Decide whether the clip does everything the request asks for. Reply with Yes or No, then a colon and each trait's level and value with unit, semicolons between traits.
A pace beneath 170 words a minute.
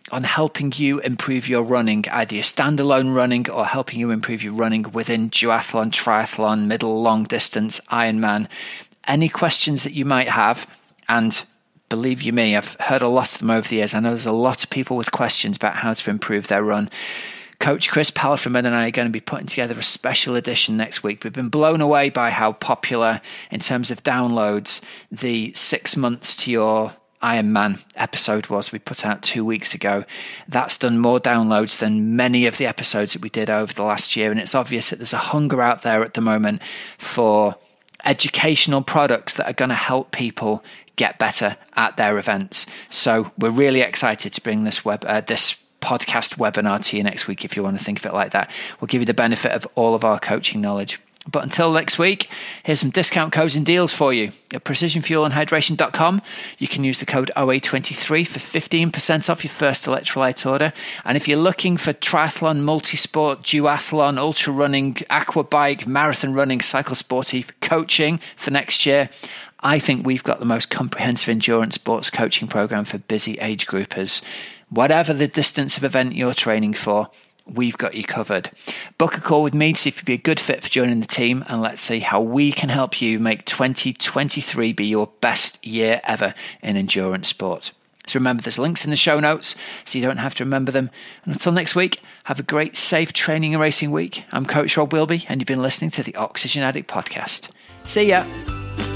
No: average, 200 wpm